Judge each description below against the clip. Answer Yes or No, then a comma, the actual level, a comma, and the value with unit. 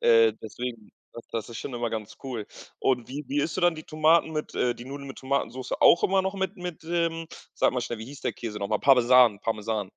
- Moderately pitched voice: No, low, 125 Hz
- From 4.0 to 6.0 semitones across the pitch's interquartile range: Yes, wide, 5.5 semitones